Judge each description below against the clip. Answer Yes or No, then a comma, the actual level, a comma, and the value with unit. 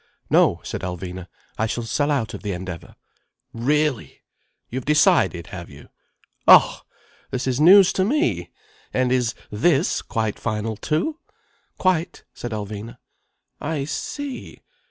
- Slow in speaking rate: Yes, slow, 130 wpm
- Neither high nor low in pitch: No, low, 125 Hz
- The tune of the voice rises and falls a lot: Yes, wide, 6.6 semitones